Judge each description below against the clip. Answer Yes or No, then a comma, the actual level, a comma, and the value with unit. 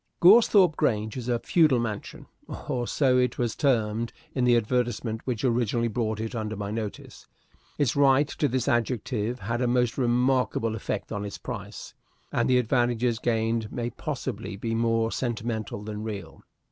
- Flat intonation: Yes, narrow, 2.3 semitones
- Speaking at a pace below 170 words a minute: Yes, average, 160 wpm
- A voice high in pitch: No, low, 120 Hz